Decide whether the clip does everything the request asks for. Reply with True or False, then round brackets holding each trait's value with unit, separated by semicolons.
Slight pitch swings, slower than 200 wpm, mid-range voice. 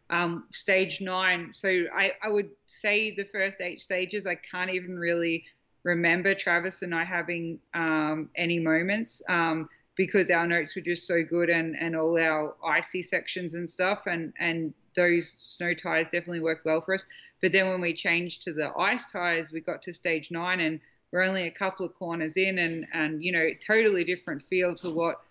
True (2.0 semitones; 190 wpm; 175 Hz)